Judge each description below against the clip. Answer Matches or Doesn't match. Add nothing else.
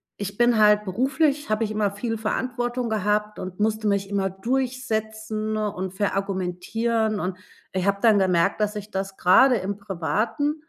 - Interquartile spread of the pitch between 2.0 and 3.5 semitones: Matches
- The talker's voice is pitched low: Doesn't match